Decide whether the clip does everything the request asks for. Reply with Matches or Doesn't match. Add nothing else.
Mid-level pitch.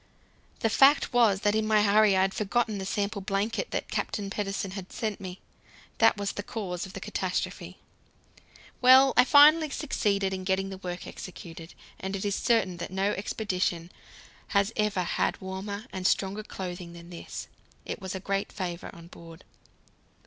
Doesn't match